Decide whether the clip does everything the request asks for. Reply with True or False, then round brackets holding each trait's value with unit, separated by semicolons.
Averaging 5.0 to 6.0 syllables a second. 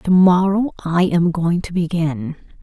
False (4.0 syllables/s)